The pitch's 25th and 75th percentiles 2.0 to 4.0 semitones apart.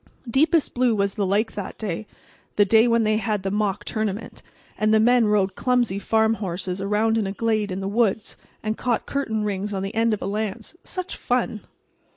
Yes: narrow, 2.4 semitones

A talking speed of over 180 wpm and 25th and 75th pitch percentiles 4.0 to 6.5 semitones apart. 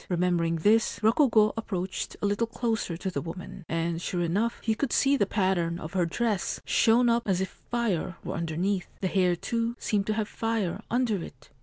Yes: average, 195 wpm; average, 4.5 semitones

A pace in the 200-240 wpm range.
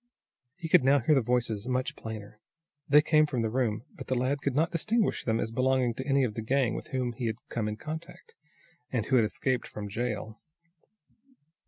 Yes: fast, 205 wpm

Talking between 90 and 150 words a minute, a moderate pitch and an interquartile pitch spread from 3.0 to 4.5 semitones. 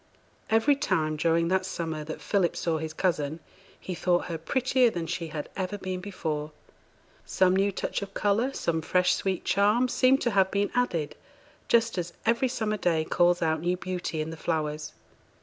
No: average, 180 wpm; medium, 180 Hz; average, 4.0 semitones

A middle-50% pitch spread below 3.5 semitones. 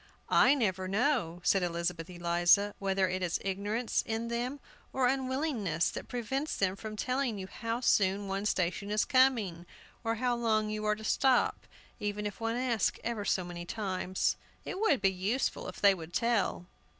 No: average, 4.2 semitones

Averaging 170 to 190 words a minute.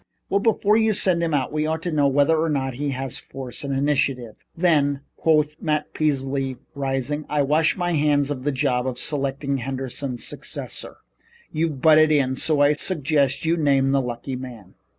Yes: average, 180 wpm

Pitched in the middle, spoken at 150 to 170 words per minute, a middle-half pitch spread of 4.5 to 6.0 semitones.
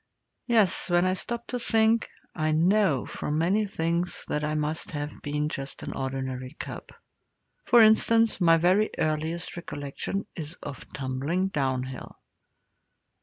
No: medium, 165 Hz; slow, 135 wpm; average, 5.0 semitones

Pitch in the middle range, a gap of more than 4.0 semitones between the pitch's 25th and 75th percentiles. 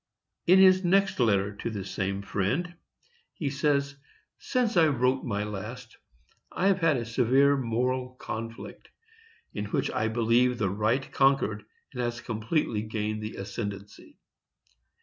No: low, 120 Hz; average, 4.8 semitones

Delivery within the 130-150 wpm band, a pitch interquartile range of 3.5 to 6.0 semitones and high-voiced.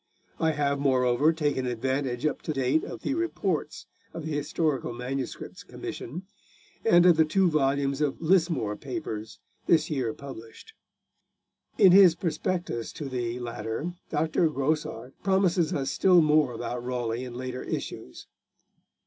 No: average, 140 wpm; average, 4.4 semitones; medium, 145 Hz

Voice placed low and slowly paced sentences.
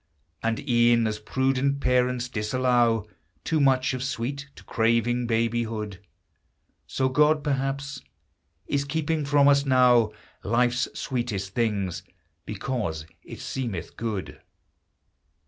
Yes: low, 125 Hz; slow, 110 wpm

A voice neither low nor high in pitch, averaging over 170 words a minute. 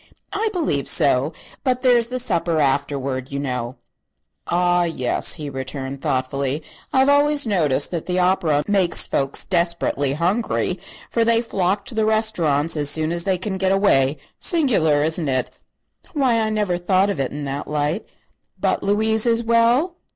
No: medium, 175 Hz; average, 165 wpm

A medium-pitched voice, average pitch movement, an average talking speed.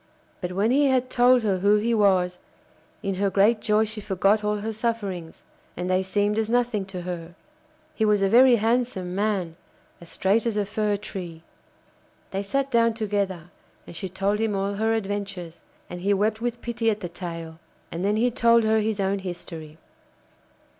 No: high, 205 Hz; average, 3.1 semitones; average, 185 wpm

